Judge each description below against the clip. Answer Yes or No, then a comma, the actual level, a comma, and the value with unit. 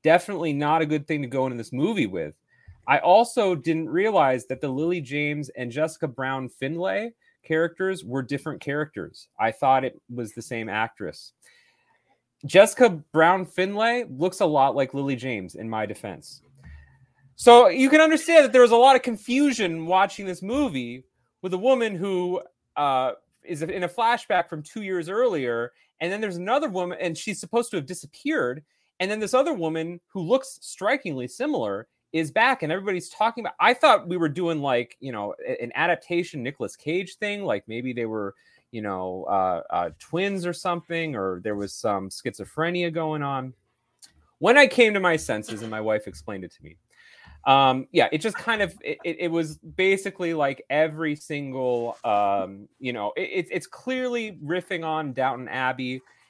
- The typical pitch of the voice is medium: Yes, medium, 160 Hz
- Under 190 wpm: Yes, average, 175 wpm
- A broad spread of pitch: Yes, wide, 7.2 semitones